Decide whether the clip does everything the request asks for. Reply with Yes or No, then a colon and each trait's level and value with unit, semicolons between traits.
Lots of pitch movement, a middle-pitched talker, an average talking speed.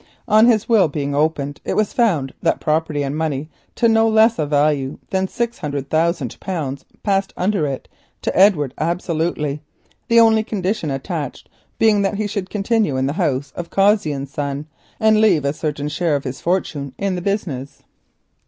Yes: wide, 6.2 semitones; medium, 165 Hz; average, 170 wpm